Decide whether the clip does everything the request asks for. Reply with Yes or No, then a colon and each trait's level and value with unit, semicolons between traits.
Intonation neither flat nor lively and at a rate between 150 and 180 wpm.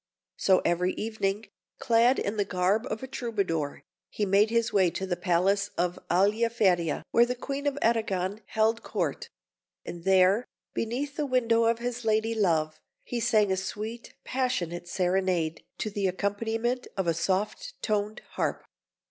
Yes: average, 3.8 semitones; average, 155 wpm